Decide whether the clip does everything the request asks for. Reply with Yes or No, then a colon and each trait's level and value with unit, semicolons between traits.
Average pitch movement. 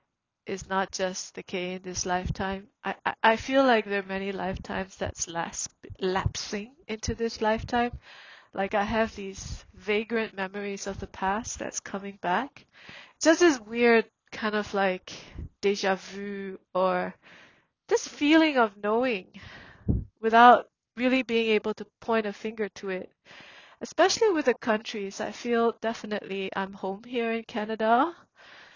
Yes: average, 3.2 semitones